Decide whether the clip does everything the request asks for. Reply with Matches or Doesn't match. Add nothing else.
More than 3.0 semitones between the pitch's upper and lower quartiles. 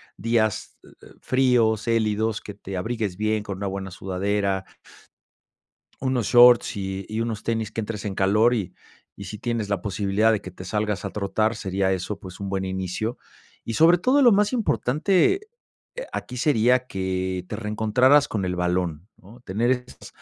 Matches